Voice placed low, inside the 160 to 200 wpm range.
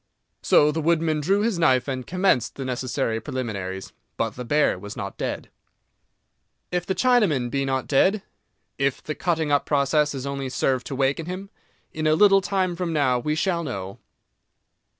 No: medium, 145 Hz; average, 170 wpm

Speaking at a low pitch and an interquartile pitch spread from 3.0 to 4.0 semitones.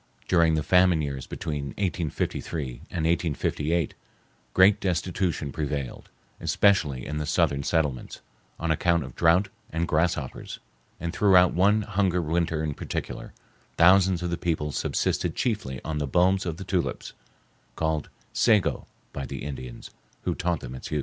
Yes: very low, 85 Hz; average, 3.4 semitones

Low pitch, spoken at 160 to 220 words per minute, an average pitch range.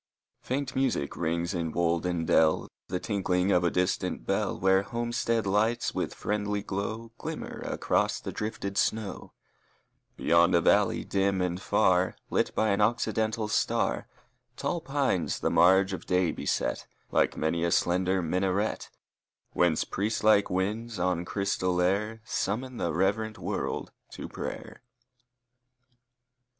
No: very low, 95 Hz; average, 140 wpm; average, 3.5 semitones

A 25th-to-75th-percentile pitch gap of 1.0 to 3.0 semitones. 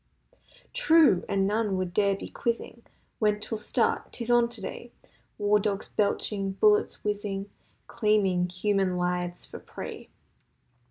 Yes: narrow, 2.6 semitones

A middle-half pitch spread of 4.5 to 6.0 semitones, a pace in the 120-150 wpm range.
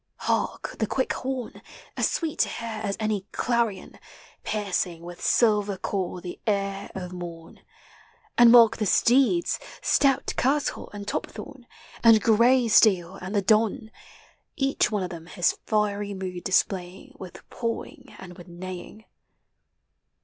No: average, 3.9 semitones; average, 140 wpm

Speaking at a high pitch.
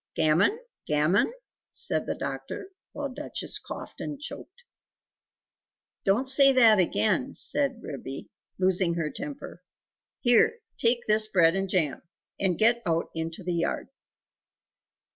Yes: high, 210 Hz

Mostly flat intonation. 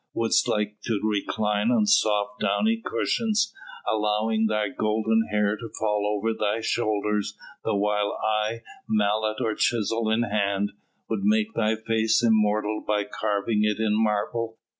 Yes: narrow, 1.3 semitones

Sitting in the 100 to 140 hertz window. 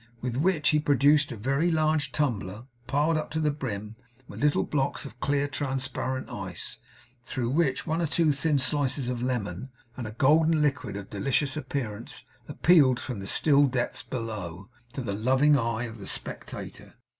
Yes: low, 135 Hz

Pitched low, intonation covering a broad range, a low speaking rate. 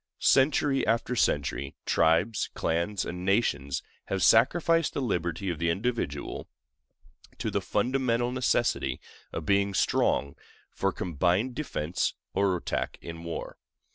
Yes: very low, 95 Hz; wide, 6.5 semitones; slow, 120 wpm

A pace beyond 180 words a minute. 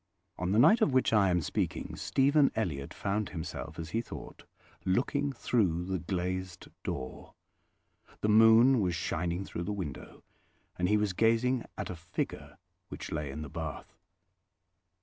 No: average, 155 wpm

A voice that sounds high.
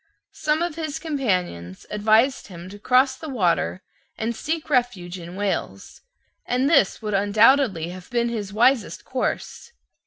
Yes: high, 225 Hz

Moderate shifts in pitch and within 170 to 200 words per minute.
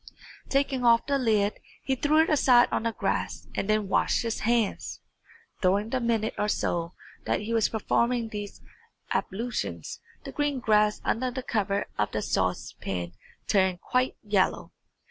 No: average, 3.4 semitones; average, 155 wpm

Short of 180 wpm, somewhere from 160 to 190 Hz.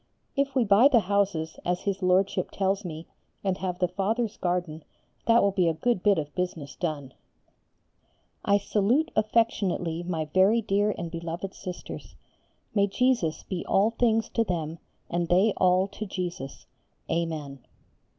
Yes: average, 150 wpm; medium, 185 Hz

